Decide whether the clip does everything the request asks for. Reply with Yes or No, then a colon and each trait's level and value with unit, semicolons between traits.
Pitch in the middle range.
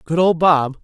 Yes: medium, 160 Hz